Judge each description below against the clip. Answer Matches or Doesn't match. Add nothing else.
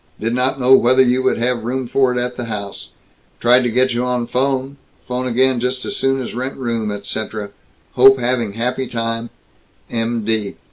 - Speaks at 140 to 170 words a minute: Doesn't match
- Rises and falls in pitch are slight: Matches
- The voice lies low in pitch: Matches